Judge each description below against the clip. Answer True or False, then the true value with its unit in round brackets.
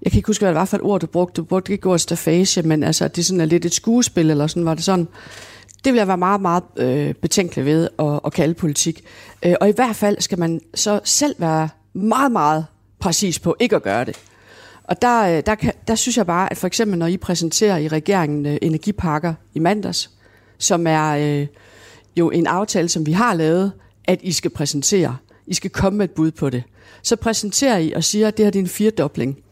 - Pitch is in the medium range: True (170 Hz)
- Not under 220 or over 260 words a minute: True (225 wpm)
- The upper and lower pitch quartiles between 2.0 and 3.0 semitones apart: False (4.3 semitones)